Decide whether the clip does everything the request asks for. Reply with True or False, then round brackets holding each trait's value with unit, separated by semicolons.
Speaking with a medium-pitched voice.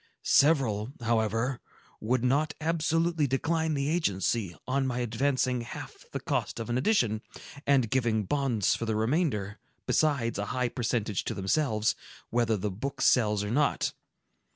False (120 Hz)